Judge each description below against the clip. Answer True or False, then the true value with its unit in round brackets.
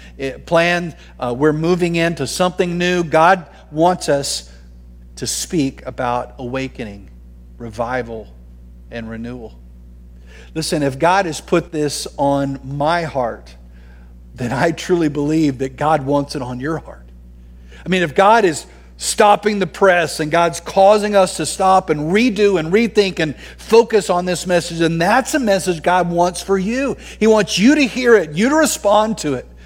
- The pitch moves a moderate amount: False (7.1 semitones)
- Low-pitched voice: False (160 Hz)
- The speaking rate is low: False (160 wpm)